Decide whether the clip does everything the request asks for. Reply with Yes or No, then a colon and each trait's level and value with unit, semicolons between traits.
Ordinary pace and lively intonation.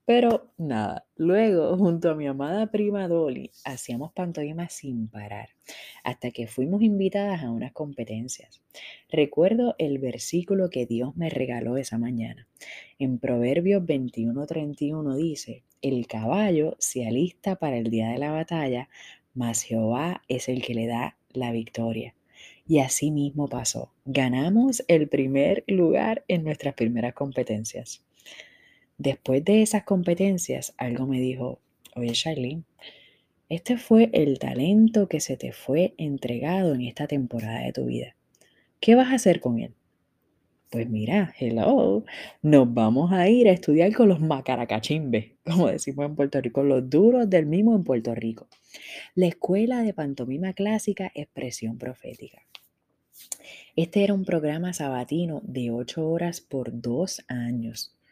Yes: average, 140 wpm; wide, 6.5 semitones